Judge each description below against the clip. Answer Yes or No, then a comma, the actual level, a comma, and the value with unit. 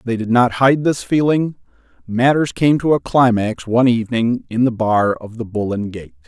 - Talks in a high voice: No, low, 120 Hz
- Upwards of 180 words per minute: Yes, average, 200 wpm